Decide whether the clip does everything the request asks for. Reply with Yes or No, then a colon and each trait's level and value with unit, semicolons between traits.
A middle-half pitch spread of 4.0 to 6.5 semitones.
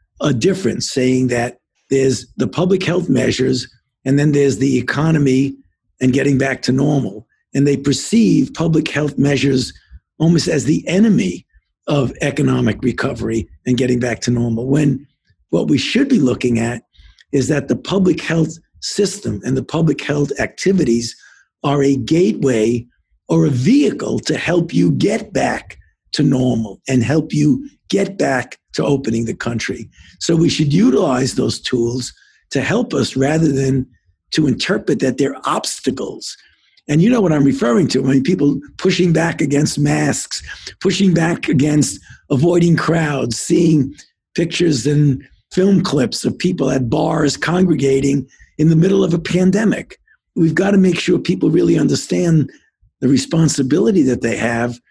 Yes: average, 4.3 semitones